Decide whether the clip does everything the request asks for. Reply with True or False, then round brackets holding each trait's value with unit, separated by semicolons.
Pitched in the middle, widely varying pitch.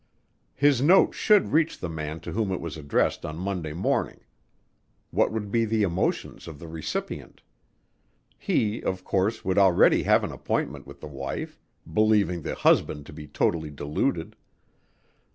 False (90 Hz; 5.8 semitones)